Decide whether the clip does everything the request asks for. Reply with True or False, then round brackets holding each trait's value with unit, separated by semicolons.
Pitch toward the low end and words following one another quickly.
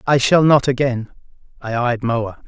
False (125 Hz; 170 wpm)